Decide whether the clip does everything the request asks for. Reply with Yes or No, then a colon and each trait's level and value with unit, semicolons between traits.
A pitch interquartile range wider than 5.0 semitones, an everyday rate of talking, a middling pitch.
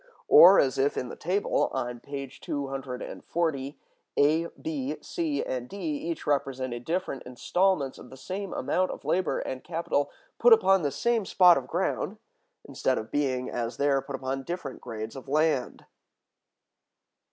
Yes: wide, 5.5 semitones; average, 150 wpm; medium, 145 Hz